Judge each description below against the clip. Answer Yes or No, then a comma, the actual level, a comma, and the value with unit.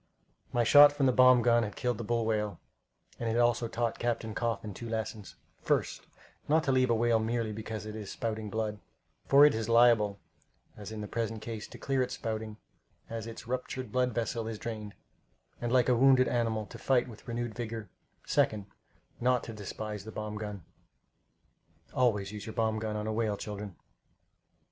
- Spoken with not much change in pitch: Yes, narrow, 2.0 semitones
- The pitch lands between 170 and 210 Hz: No, low, 115 Hz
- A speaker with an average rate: Yes, average, 190 wpm